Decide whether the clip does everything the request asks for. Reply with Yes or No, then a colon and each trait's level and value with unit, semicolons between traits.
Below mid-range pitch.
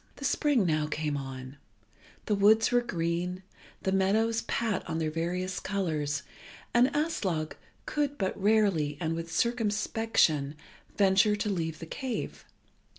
No: high, 190 Hz